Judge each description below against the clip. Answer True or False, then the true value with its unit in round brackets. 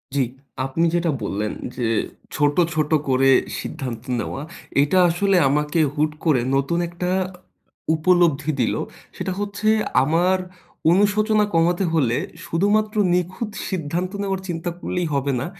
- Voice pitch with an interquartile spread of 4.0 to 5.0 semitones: True (4.5 semitones)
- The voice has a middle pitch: True (165 Hz)